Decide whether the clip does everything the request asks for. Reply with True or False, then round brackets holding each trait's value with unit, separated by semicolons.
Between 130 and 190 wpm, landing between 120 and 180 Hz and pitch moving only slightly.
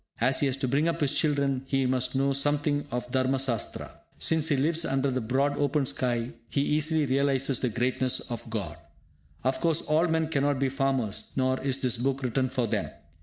False (200 wpm; 135 Hz; 2.1 semitones)